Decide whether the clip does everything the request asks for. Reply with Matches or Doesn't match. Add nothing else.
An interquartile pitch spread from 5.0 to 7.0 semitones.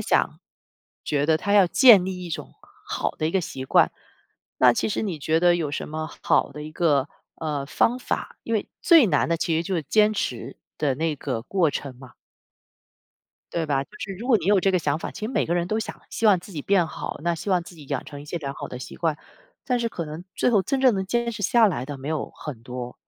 Matches